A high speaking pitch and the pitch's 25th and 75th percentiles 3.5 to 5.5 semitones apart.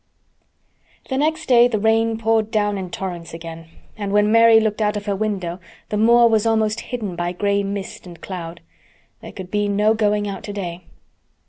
No: high, 205 Hz; average, 2.7 semitones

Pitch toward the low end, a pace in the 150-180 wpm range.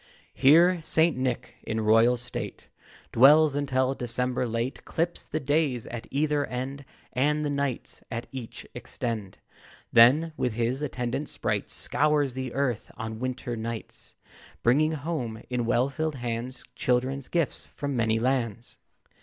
No: low, 130 Hz; slow, 135 wpm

